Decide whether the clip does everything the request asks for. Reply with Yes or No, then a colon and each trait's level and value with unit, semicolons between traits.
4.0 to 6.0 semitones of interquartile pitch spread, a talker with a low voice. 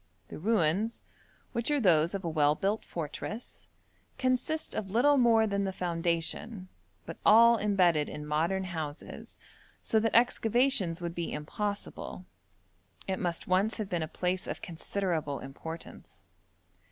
No: average, 5.0 semitones; high, 190 Hz